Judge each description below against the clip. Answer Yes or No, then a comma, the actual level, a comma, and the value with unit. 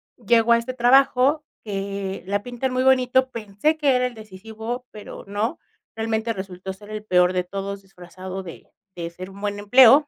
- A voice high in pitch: Yes, high, 215 Hz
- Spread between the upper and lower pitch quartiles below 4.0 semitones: No, average, 4.4 semitones